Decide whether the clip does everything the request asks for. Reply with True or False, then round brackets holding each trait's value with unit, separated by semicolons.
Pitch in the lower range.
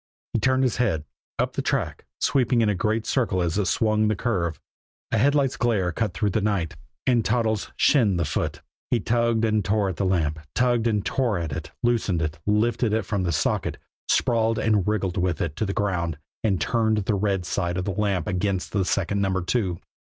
True (105 Hz)